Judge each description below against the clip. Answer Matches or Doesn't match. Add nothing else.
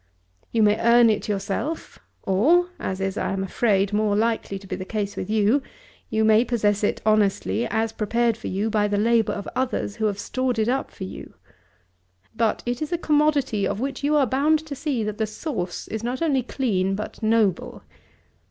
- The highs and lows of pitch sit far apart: Doesn't match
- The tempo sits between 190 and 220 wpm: Matches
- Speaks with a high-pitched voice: Matches